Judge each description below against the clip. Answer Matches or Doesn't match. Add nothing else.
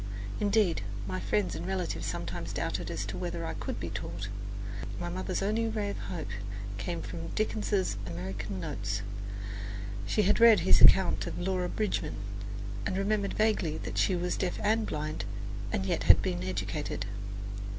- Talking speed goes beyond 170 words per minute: Doesn't match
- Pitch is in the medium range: Matches